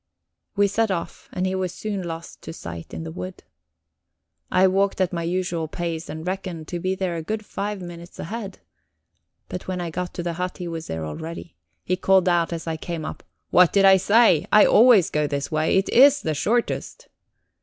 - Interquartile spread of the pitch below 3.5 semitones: Yes, average, 2.7 semitones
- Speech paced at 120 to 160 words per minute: No, fast, 205 wpm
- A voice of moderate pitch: Yes, medium, 180 Hz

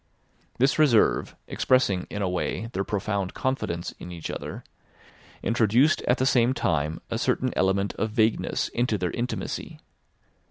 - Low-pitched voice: Yes, low, 110 Hz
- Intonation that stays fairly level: No, average, 4.6 semitones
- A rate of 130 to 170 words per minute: Yes, average, 145 wpm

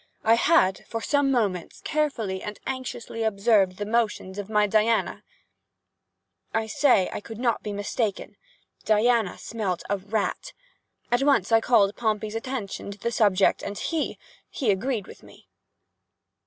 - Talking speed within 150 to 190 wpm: No, average, 140 wpm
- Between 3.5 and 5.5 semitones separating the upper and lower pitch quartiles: No, average, 3.0 semitones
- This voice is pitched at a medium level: No, high, 220 Hz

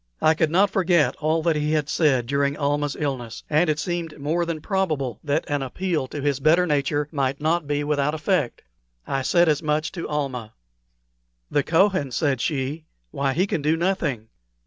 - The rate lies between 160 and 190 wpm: Yes, average, 185 wpm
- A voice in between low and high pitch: Yes, medium, 150 Hz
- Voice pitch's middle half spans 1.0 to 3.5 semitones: Yes, average, 2.8 semitones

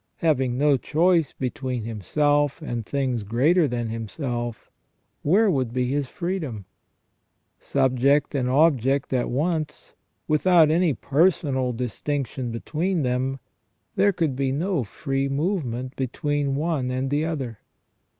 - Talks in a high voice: No, low, 135 Hz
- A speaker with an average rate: No, slow, 125 wpm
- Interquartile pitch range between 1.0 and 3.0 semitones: No, average, 3.6 semitones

